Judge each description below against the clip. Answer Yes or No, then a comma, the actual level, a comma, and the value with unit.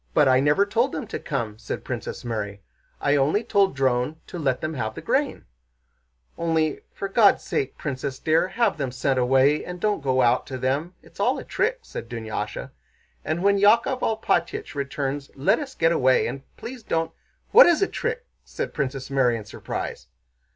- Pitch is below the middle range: No, medium, 145 Hz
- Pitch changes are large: Yes, wide, 7.4 semitones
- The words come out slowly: No, average, 185 wpm